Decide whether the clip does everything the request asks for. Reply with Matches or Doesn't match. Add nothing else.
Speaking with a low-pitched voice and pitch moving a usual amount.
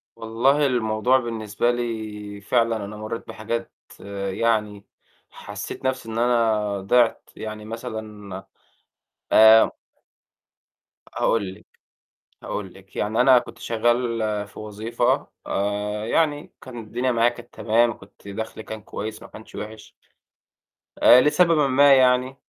Doesn't match